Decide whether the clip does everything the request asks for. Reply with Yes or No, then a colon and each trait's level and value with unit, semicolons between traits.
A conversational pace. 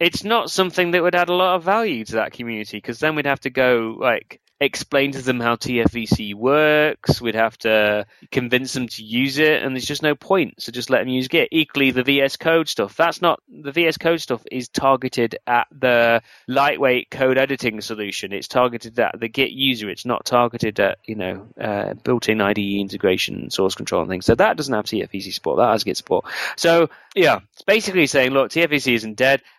No: fast, 210 wpm